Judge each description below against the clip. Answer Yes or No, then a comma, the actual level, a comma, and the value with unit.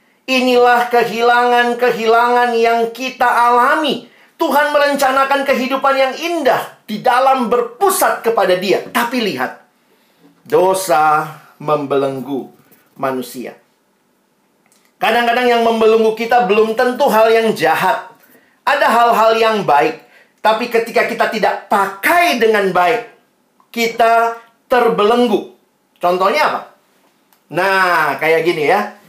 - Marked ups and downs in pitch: No, average, 2.8 semitones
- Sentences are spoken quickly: No, average, 100 wpm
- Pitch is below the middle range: No, high, 230 Hz